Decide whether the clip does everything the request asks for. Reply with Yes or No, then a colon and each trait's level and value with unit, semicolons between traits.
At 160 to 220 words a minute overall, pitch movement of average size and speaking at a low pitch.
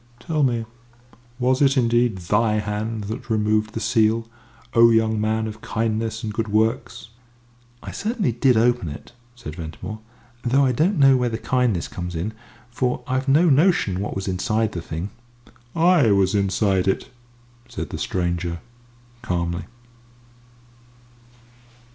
No: average, 140 wpm; average, 3.8 semitones; low, 110 Hz